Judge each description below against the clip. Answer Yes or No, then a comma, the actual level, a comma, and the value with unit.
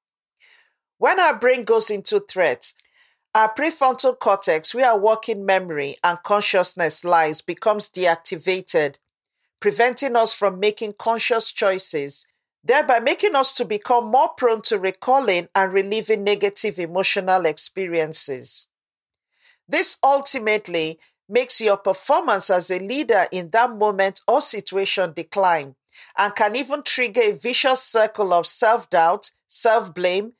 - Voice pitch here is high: Yes, high, 215 Hz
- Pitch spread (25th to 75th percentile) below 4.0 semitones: No, average, 4.8 semitones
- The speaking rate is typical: No, slow, 120 wpm